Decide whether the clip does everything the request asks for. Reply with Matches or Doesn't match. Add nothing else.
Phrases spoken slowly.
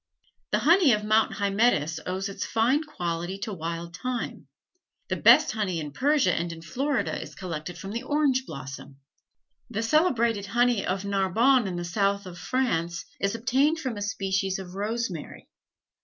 Doesn't match